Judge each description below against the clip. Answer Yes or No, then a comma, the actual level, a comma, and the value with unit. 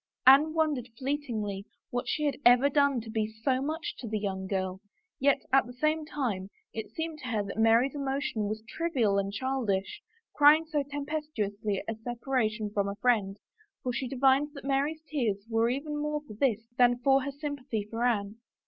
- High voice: Yes, very high, 250 Hz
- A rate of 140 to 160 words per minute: No, average, 190 wpm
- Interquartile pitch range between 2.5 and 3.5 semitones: No, average, 4.9 semitones